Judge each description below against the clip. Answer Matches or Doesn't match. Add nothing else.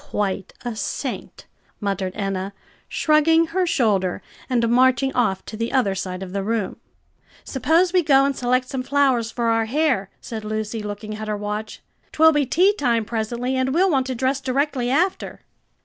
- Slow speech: Doesn't match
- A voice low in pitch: Doesn't match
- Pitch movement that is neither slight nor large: Matches